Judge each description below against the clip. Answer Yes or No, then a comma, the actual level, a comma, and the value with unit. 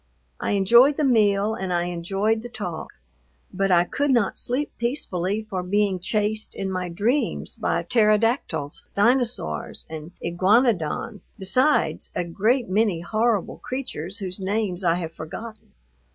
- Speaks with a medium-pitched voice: No, high, 205 Hz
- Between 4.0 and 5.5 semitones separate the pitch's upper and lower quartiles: Yes, average, 4.4 semitones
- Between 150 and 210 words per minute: No, slow, 135 wpm